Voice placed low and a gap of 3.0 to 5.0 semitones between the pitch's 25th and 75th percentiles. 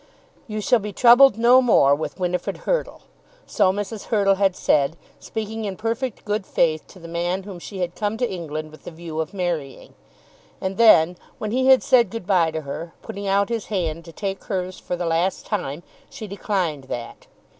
No: high, 190 Hz; average, 4.3 semitones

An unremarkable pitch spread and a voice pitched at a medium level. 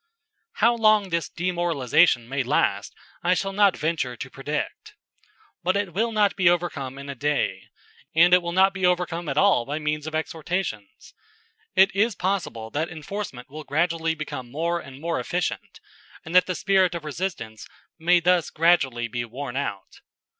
Yes: average, 4.6 semitones; medium, 165 Hz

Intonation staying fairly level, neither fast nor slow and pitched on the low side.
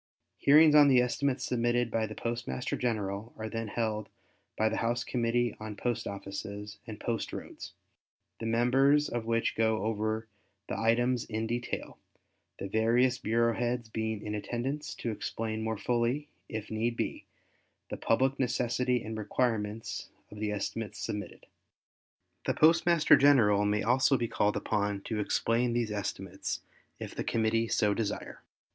Yes: narrow, 2.1 semitones; average, 150 wpm; low, 115 Hz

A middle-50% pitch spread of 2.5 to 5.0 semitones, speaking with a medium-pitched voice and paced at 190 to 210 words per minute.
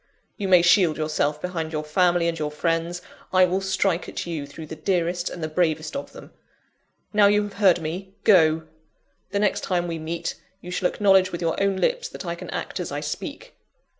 Yes: average, 3.0 semitones; medium, 175 Hz; fast, 205 wpm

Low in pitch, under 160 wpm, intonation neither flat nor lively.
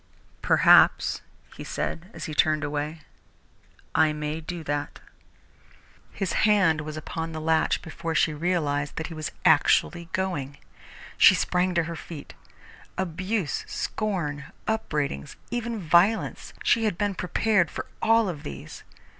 No: medium, 165 Hz; slow, 135 wpm; average, 3.7 semitones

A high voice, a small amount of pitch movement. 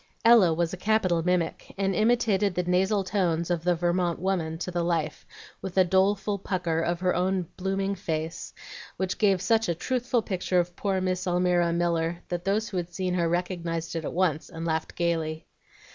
No: medium, 180 Hz; narrow, 2.2 semitones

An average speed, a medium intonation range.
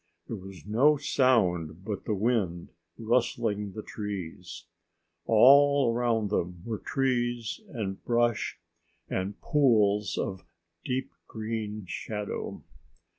No: slow, 105 wpm; average, 3.6 semitones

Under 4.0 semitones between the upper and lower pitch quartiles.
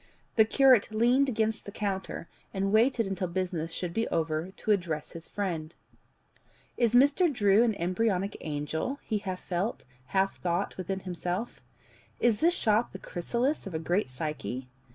No: average, 4.7 semitones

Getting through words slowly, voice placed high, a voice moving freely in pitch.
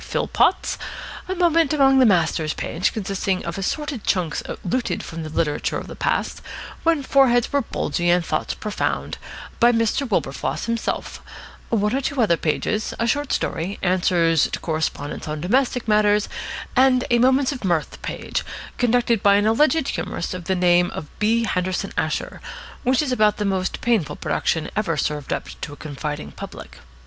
No: average, 165 wpm; high, 210 Hz; wide, 6.8 semitones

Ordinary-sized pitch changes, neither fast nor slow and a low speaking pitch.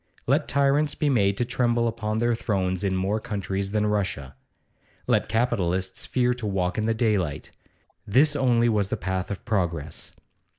Yes: average, 3.9 semitones; average, 165 wpm; low, 105 Hz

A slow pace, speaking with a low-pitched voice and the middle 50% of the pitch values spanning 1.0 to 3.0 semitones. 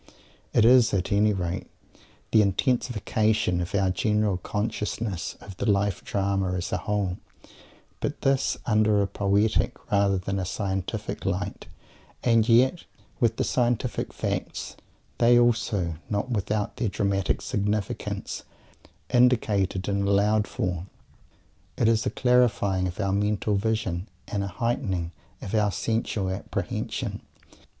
Yes: slow, 130 wpm; low, 105 Hz; narrow, 2.5 semitones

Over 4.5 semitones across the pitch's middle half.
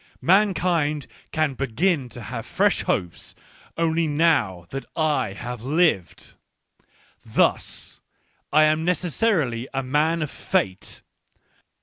Yes: average, 5.2 semitones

